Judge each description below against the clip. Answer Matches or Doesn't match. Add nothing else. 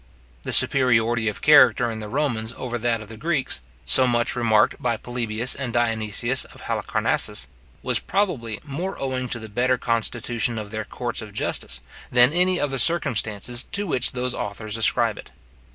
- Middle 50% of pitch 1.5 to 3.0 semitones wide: Matches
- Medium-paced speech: Matches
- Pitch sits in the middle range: Doesn't match